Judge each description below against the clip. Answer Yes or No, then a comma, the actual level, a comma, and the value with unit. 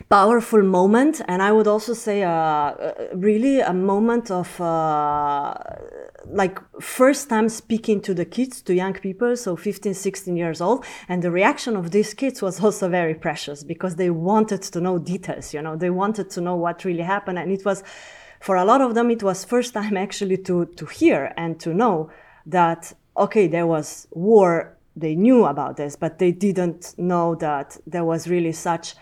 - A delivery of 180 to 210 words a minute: Yes, average, 185 wpm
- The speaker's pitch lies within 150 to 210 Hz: Yes, high, 190 Hz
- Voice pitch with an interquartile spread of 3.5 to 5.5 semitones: Yes, average, 4.1 semitones